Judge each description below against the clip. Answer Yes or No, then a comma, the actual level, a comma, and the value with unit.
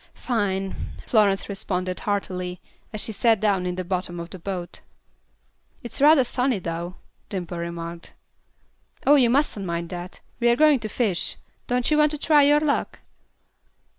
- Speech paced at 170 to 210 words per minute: No, average, 155 wpm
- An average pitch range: No, wide, 5.7 semitones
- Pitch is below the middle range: No, high, 200 Hz